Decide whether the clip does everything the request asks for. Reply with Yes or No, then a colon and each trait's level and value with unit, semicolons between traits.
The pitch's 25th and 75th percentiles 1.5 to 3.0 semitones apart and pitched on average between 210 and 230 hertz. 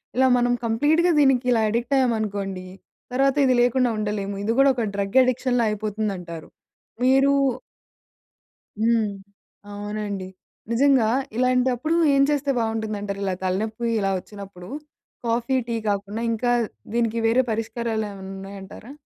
No: average, 3.7 semitones; high, 225 Hz